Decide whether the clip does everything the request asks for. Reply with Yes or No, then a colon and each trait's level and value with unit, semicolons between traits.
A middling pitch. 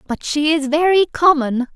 No: very high, 300 Hz